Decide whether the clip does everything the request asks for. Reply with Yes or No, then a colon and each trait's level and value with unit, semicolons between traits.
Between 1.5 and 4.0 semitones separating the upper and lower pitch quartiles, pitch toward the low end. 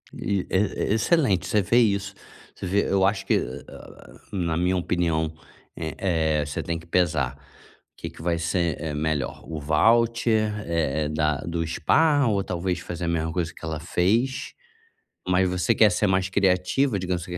Yes: average, 3.7 semitones; very low, 90 Hz